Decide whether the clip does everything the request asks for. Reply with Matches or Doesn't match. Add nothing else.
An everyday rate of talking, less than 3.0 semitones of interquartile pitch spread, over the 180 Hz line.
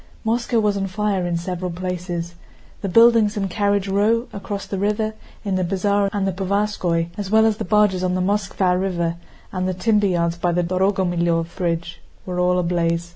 Matches